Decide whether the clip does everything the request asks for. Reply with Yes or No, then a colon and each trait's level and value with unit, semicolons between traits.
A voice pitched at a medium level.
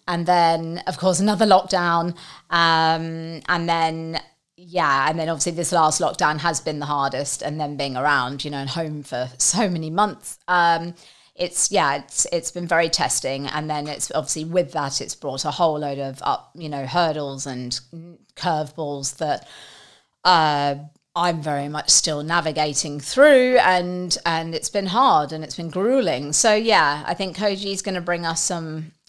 Yes: medium, 165 Hz